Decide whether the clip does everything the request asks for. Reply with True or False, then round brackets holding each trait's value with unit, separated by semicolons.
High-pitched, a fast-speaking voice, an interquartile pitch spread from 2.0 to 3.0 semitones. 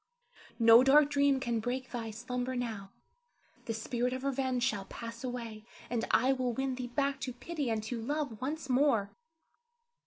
False (250 Hz; 165 wpm; 2.6 semitones)